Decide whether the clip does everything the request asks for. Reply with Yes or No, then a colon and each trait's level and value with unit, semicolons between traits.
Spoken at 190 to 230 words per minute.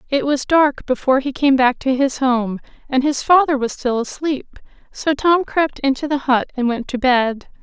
Yes: fast, 205 wpm